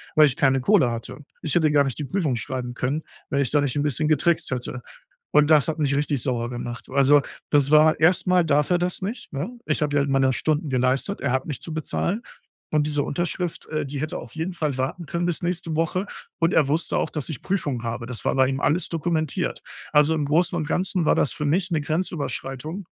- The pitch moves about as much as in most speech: Yes, average, 3.5 semitones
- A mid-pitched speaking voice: Yes, medium, 150 Hz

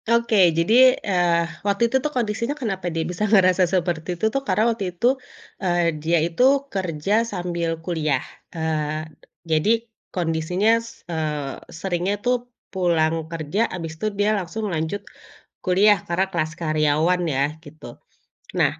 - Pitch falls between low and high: Yes, medium, 175 Hz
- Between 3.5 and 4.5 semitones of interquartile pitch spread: Yes, average, 3.9 semitones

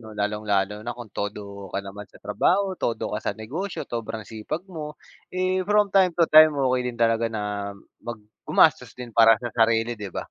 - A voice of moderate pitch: No, low, 115 Hz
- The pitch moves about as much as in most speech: No, wide, 6.4 semitones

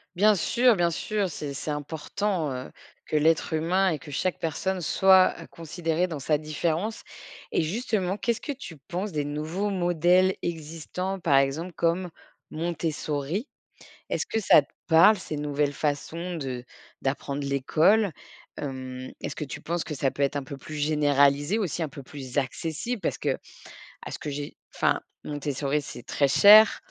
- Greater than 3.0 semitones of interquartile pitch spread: Yes, average, 4.2 semitones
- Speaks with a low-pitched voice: No, medium, 160 Hz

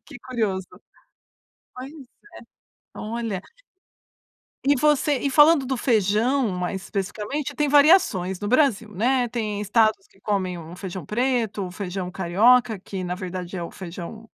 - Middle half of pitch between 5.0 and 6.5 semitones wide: Yes, average, 5.3 semitones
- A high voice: Yes, high, 210 Hz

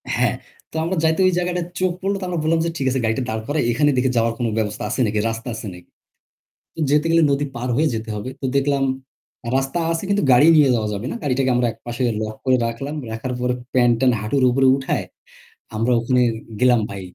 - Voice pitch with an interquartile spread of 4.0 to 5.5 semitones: Yes, average, 4.4 semitones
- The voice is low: Yes, low, 130 Hz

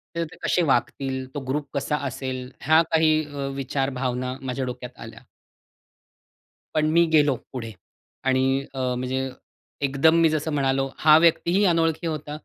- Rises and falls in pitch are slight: No, average, 3.1 semitones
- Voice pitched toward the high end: No, medium, 140 Hz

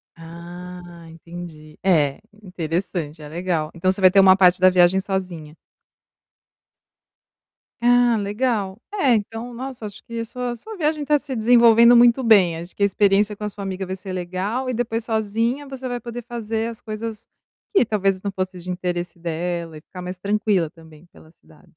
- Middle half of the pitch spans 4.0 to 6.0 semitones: Yes, average, 4.7 semitones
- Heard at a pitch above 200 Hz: No, high, 195 Hz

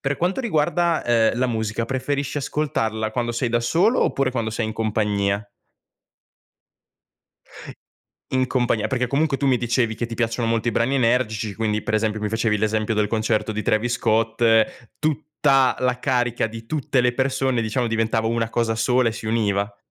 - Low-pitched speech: Yes, low, 115 Hz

